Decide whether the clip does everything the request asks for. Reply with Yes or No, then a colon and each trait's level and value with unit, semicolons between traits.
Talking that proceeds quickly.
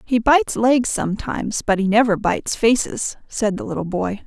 No: average, 185 wpm